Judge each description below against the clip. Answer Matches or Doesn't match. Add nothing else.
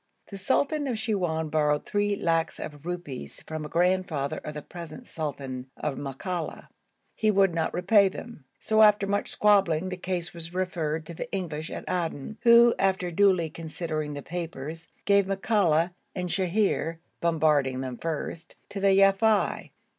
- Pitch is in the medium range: Matches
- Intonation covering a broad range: Doesn't match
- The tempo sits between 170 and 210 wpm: Doesn't match